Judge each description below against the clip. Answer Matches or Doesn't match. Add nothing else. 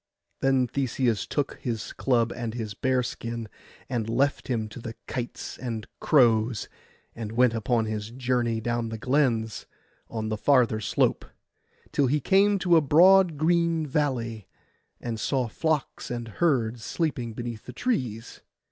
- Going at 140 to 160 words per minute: Matches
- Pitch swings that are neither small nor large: Matches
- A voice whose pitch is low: Matches